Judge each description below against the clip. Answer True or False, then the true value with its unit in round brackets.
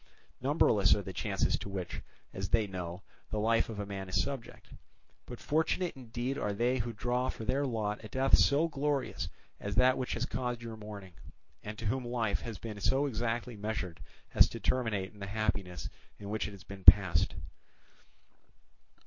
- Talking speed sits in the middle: True (180 wpm)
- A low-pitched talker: True (110 Hz)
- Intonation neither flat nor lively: True (3.7 semitones)